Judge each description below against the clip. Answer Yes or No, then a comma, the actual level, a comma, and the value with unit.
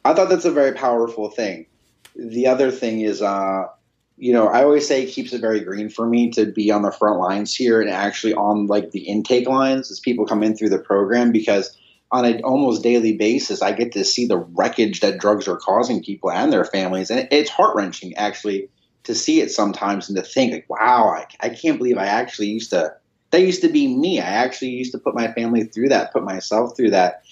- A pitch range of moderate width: Yes, average, 3.7 semitones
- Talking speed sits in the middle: No, fast, 230 wpm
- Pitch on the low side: Yes, low, 115 Hz